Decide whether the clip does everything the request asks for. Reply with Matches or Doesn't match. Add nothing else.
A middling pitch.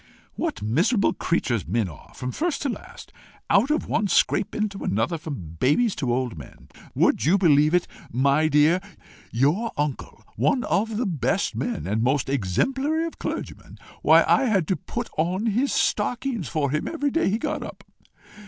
Matches